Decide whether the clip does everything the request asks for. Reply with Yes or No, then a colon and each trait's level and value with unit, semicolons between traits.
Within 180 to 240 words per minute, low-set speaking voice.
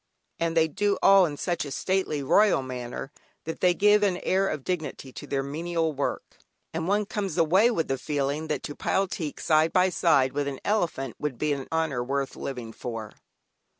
No: average, 195 wpm; medium, 155 Hz